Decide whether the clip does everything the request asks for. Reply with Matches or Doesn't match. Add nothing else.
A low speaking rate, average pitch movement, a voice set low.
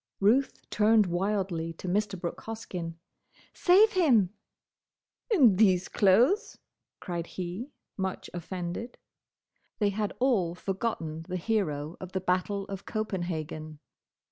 Doesn't match